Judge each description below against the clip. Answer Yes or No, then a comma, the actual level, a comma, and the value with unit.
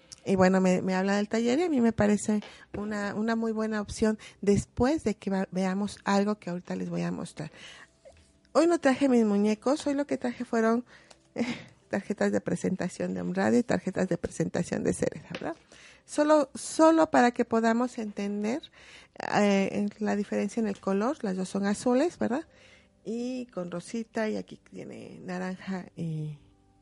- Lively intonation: No, average, 3.9 semitones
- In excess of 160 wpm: Yes, average, 170 wpm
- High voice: Yes, high, 210 Hz